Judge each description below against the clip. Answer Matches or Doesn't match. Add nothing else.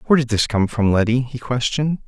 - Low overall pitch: Matches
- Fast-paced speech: Matches